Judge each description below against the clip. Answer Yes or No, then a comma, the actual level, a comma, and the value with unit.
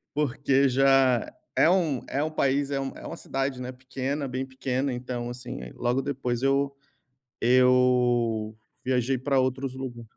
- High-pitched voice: No, low, 130 Hz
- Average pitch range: No, narrow, 1.7 semitones